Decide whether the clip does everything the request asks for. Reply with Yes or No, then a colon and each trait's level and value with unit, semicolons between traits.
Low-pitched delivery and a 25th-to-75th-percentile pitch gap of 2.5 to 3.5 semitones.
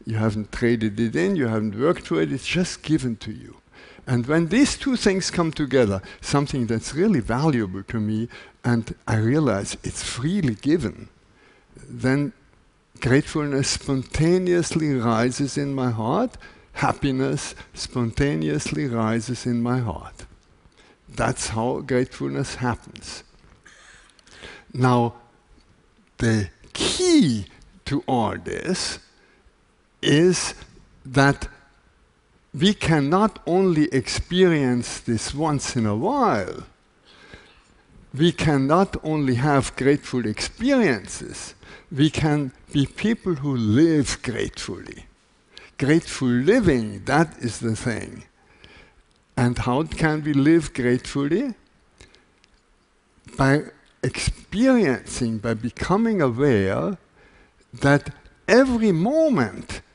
No: low, 130 Hz; average, 5.3 semitones